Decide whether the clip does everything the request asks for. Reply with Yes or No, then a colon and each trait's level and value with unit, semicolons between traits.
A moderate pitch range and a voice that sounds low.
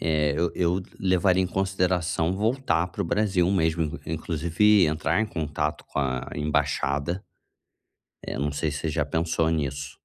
Yes: average, 3.5 semitones; very low, 80 Hz